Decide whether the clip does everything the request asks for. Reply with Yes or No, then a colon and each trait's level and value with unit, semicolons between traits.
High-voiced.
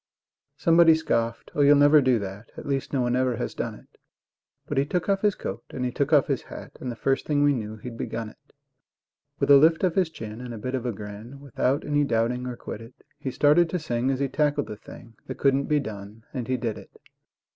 No: low, 130 Hz